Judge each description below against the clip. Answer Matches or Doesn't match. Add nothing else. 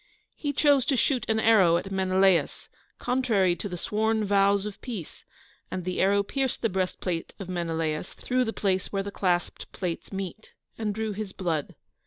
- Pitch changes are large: Doesn't match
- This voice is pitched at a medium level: Doesn't match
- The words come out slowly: Doesn't match